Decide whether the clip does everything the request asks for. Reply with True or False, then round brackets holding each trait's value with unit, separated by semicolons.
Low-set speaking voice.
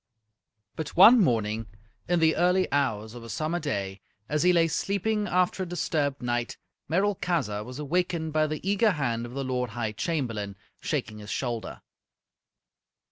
False (145 Hz)